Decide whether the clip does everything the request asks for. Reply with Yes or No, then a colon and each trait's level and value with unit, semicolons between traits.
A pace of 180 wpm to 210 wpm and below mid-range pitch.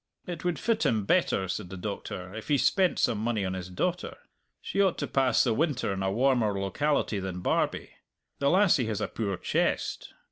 Yes: average, 200 wpm; low, 115 Hz